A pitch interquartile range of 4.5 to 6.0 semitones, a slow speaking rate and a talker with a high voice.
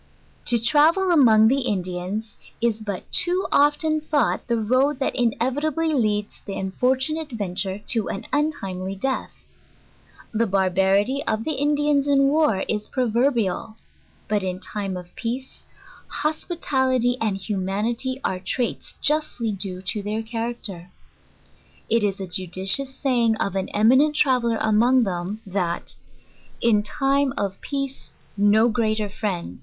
Yes: wide, 5.4 semitones; slow, 130 wpm; high, 225 Hz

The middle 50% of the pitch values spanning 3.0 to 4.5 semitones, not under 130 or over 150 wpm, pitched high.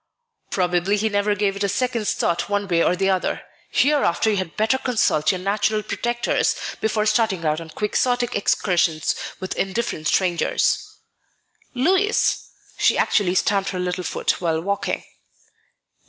Yes: average, 3.5 semitones; average, 145 wpm; high, 200 Hz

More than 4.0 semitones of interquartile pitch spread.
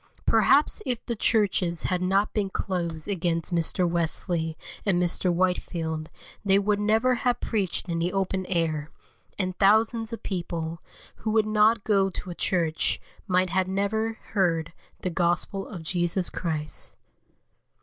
No: average, 3.5 semitones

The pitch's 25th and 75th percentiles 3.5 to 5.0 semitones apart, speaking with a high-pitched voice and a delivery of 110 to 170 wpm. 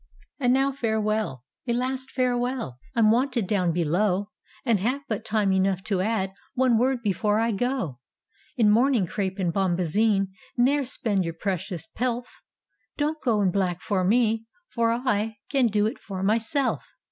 Yes: average, 4.4 semitones; high, 220 Hz; average, 165 wpm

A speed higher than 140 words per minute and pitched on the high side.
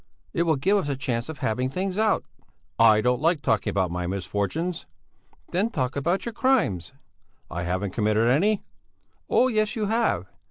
No: average, 170 wpm; medium, 140 Hz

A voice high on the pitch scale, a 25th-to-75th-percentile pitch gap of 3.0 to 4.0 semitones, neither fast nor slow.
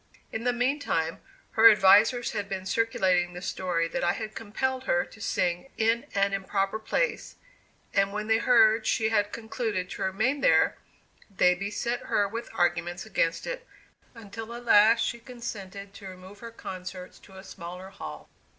Yes: high, 205 Hz; average, 3.5 semitones; average, 170 wpm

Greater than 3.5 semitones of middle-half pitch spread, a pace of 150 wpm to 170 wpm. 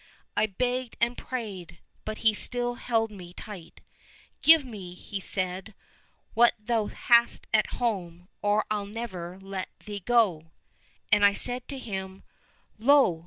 Yes: average, 4.1 semitones; average, 165 wpm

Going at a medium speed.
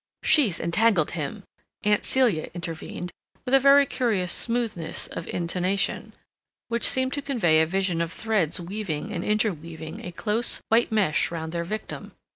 Yes: average, 150 wpm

